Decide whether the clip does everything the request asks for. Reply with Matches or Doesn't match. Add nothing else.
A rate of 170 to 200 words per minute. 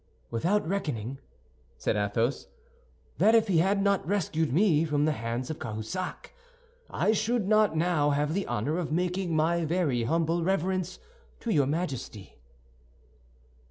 Doesn't match